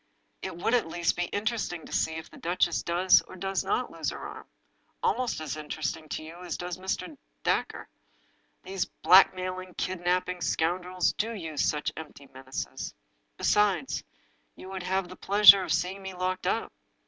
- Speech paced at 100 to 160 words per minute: No, average, 170 wpm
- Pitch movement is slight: Yes, narrow, 2.2 semitones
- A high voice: No, medium, 180 Hz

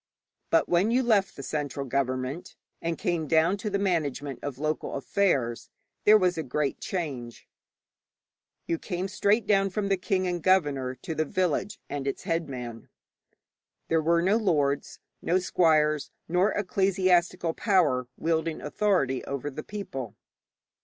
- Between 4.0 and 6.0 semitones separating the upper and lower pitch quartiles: Yes, average, 5.2 semitones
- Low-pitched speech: No, medium, 165 Hz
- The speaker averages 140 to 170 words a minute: Yes, average, 145 wpm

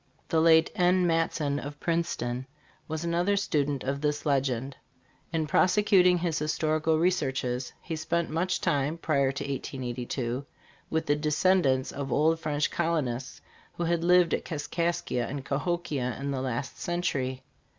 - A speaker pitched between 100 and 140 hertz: No, medium, 150 Hz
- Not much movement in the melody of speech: No, average, 3.8 semitones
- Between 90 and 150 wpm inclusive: Yes, average, 140 wpm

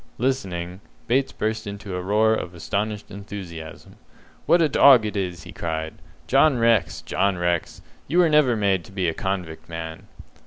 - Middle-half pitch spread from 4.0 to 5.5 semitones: Yes, average, 4.8 semitones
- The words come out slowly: No, average, 165 wpm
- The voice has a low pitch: Yes, low, 100 Hz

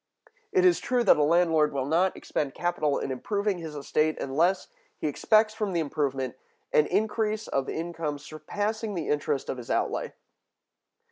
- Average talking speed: Yes, average, 160 wpm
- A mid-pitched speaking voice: Yes, medium, 165 Hz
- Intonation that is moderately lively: No, wide, 6.0 semitones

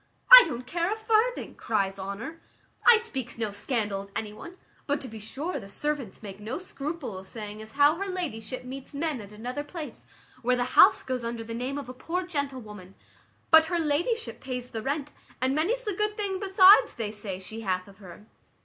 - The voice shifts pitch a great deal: Yes, wide, 7.6 semitones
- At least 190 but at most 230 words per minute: Yes, fast, 205 wpm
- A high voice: Yes, very high, 260 Hz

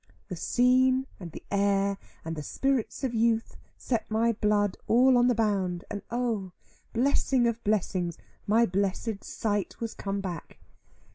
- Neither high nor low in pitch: No, high, 215 Hz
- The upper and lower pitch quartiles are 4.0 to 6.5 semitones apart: No, average, 3.4 semitones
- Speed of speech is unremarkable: Yes, average, 150 wpm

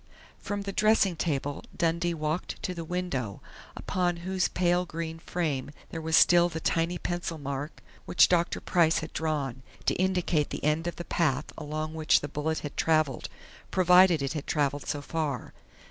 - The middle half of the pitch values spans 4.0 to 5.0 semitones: No, average, 2.8 semitones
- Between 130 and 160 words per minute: No, average, 170 wpm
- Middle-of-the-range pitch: Yes, medium, 165 Hz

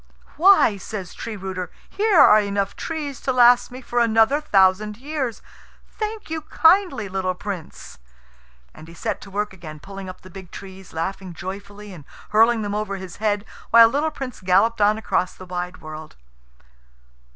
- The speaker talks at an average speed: Yes, average, 170 wpm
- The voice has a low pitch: No, high, 205 Hz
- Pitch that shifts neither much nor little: Yes, average, 4.5 semitones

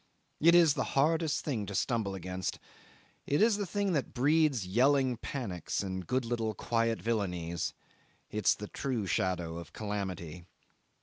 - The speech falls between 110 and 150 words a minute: Yes, average, 145 wpm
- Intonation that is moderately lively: No, wide, 7.0 semitones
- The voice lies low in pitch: Yes, low, 115 Hz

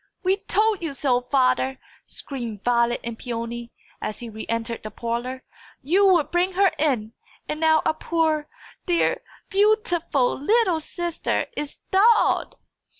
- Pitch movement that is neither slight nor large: No, wide, 6.9 semitones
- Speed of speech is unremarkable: Yes, average, 150 wpm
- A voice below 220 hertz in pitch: No, very high, 290 Hz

